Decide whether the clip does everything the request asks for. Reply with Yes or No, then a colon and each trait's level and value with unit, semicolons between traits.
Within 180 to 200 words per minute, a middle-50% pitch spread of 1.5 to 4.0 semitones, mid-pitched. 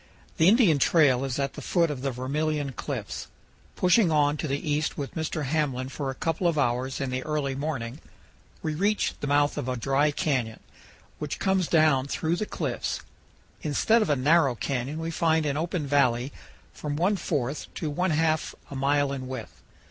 Yes: average, 185 wpm; average, 3.0 semitones; medium, 145 Hz